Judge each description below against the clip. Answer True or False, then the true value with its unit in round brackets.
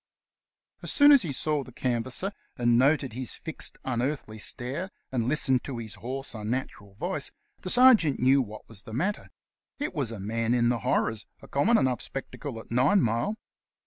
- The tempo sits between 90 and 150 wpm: False (175 wpm)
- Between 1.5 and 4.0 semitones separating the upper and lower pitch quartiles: False (4.4 semitones)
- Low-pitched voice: True (130 Hz)